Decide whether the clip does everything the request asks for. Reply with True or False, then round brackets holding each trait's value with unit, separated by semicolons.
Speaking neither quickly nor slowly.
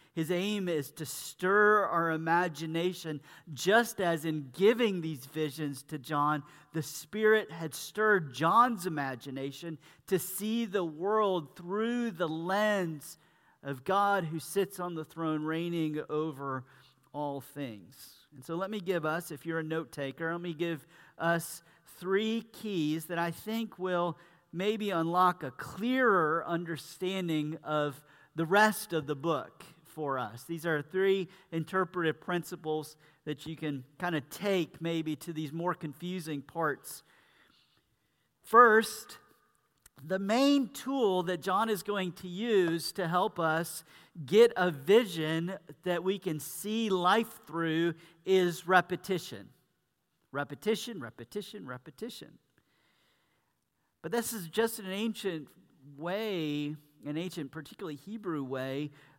False (130 wpm)